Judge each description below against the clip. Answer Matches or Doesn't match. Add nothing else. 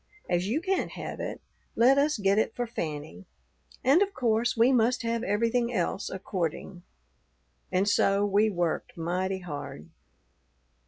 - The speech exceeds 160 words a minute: Doesn't match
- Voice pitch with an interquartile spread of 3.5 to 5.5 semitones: Matches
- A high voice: Matches